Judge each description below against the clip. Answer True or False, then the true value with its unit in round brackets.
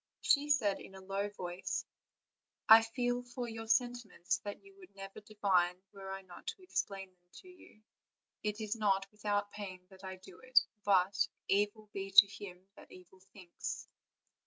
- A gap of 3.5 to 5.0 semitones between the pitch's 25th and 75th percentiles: False (2.7 semitones)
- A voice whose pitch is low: False (200 Hz)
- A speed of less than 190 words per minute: True (170 wpm)